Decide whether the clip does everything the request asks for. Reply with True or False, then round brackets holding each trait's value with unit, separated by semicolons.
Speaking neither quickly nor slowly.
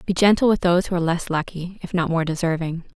False (240 wpm)